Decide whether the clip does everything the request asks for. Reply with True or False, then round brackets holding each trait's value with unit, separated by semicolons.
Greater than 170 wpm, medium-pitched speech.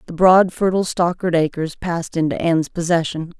False (160 wpm; 170 Hz)